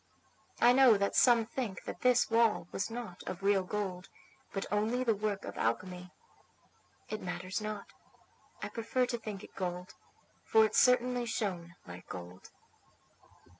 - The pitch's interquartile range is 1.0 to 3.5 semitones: No, average, 4.2 semitones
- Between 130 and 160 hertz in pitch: No, high, 210 Hz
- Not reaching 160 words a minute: Yes, average, 150 wpm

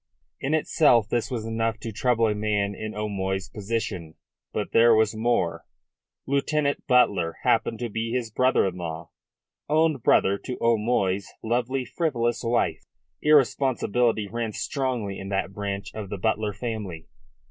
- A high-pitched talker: No, low, 110 Hz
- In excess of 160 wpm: No, average, 145 wpm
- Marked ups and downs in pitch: No, average, 3.6 semitones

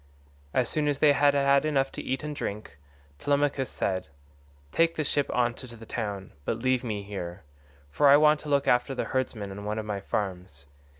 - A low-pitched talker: Yes, low, 125 Hz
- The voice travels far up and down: Yes, wide, 5.8 semitones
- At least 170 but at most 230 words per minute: Yes, average, 200 wpm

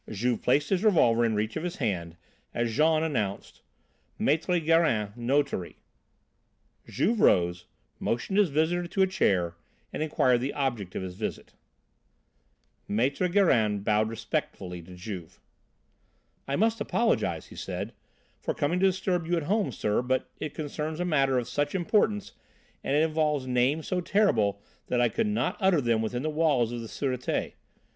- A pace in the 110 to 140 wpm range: No, average, 160 wpm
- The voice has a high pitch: No, medium, 140 Hz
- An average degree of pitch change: No, wide, 7.3 semitones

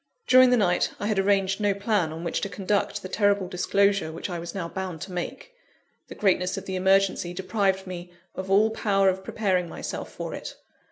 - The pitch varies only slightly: Yes, narrow, 1.9 semitones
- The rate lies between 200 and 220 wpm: Yes, fast, 205 wpm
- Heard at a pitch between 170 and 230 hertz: Yes, high, 190 Hz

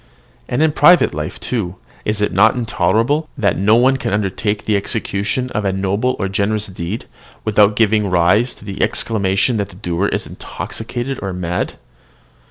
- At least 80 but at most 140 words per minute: No, average, 170 wpm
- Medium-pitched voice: No, low, 105 Hz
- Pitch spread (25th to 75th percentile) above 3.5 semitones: No, average, 3.1 semitones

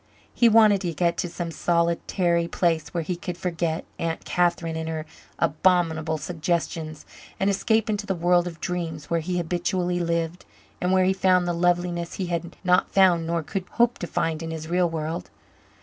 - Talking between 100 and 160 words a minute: No, average, 180 wpm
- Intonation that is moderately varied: No, narrow, 1.6 semitones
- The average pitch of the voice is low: No, medium, 175 Hz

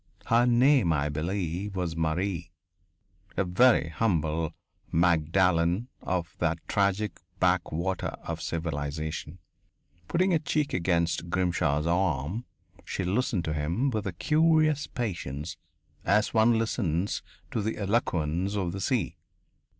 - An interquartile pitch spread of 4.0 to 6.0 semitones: Yes, average, 5.1 semitones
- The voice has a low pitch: Yes, very low, 90 Hz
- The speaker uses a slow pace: Yes, slow, 120 wpm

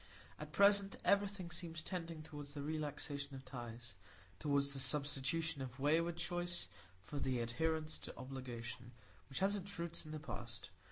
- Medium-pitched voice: Yes, medium, 145 Hz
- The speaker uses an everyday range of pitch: Yes, average, 4.6 semitones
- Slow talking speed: No, average, 150 wpm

